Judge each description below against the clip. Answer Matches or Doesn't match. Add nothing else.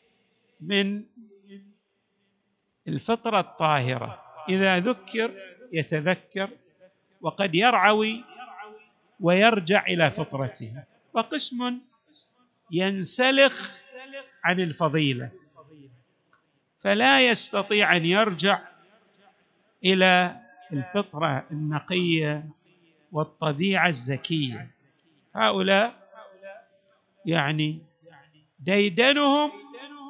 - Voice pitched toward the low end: Doesn't match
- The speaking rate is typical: Doesn't match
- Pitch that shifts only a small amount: Doesn't match